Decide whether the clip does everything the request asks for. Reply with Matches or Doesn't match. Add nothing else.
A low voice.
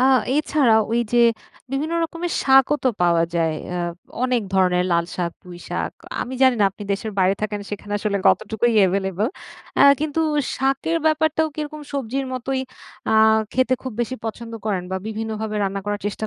Doesn't match